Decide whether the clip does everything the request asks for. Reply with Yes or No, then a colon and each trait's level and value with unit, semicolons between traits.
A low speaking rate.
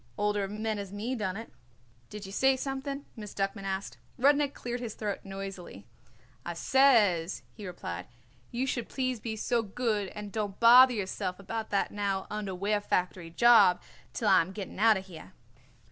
No: average, 170 wpm